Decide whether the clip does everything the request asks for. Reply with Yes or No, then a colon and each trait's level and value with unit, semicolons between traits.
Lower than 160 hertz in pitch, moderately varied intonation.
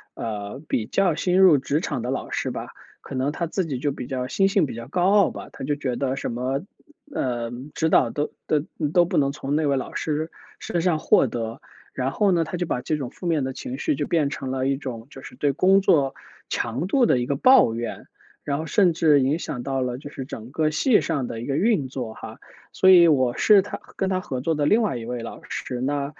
Yes: medium, 140 Hz; average, 5.0 semitones